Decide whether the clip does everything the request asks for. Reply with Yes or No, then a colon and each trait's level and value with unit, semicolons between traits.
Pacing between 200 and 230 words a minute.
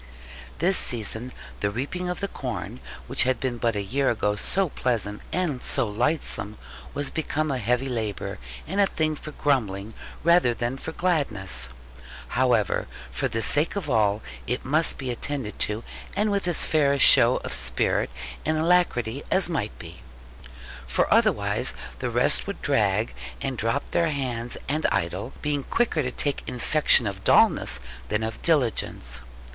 No: average, 160 wpm